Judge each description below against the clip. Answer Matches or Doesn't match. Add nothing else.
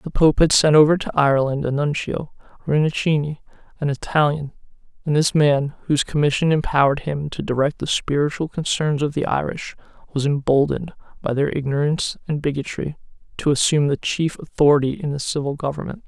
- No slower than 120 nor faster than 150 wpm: Doesn't match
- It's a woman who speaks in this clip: Doesn't match